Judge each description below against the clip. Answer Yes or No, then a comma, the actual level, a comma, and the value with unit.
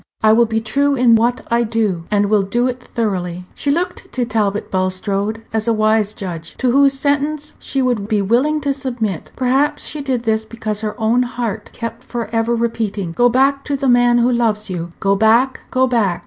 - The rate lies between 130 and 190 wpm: No, fast, 205 wpm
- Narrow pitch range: No, average, 3.2 semitones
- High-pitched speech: Yes, high, 230 Hz